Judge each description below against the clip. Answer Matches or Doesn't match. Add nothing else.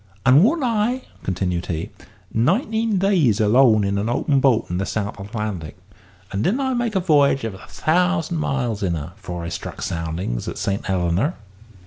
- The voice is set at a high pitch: Doesn't match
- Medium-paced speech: Matches